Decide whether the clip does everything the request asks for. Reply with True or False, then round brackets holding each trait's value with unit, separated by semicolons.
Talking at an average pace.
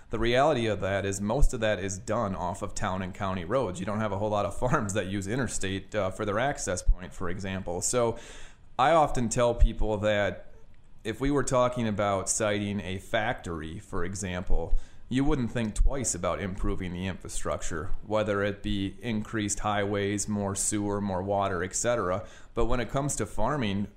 True (185 wpm)